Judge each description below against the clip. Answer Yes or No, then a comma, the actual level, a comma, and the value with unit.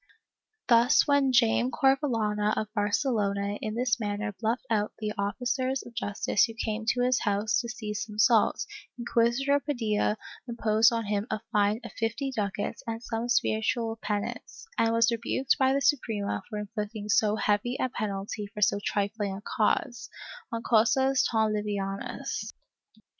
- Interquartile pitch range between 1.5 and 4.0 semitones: Yes, narrow, 2.6 semitones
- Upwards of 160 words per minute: No, average, 155 wpm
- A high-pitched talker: Yes, high, 220 Hz